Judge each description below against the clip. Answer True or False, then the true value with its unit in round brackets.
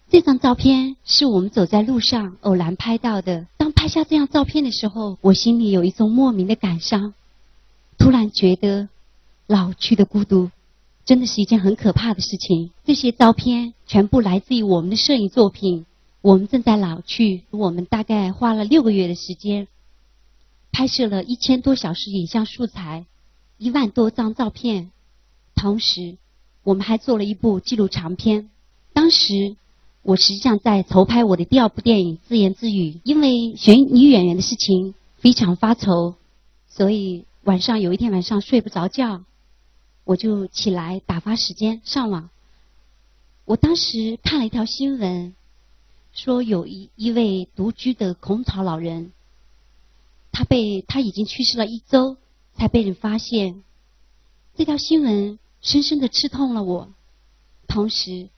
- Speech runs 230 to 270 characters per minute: True (235 characters per minute)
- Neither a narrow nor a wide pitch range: True (4.4 semitones)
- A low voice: False (205 Hz)